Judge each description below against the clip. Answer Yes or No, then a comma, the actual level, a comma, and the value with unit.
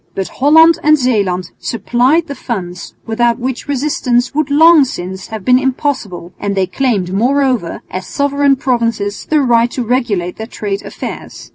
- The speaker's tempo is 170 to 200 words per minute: No, average, 155 wpm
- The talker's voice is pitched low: No, high, 245 Hz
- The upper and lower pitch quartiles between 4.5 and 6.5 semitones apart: Yes, wide, 5.6 semitones